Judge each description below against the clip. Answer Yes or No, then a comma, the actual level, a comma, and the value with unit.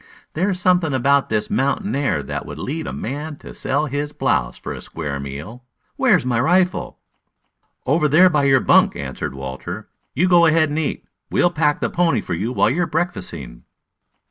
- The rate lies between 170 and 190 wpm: Yes, average, 185 wpm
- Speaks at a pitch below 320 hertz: Yes, medium, 140 Hz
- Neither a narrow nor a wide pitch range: No, wide, 7.2 semitones